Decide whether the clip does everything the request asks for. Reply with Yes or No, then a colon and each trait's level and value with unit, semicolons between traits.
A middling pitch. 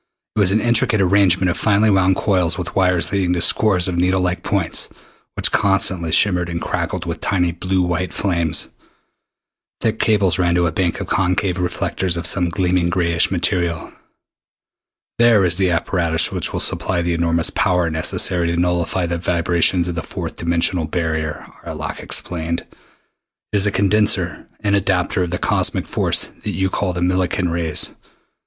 No: very low, 90 Hz